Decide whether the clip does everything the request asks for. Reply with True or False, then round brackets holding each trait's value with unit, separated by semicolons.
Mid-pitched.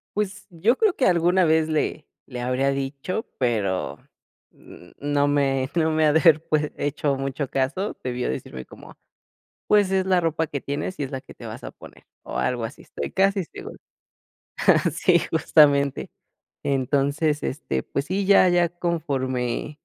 True (150 Hz)